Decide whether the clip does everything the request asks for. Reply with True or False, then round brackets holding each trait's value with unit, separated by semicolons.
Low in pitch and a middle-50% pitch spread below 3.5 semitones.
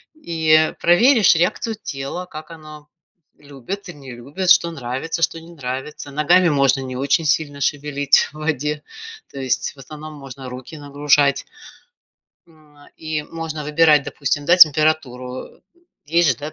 False (150 Hz; 2.8 semitones)